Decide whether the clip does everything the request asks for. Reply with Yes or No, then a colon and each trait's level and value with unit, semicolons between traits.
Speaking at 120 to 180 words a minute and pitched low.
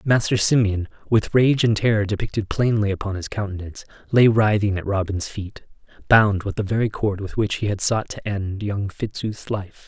No: average, 190 wpm; low, 105 Hz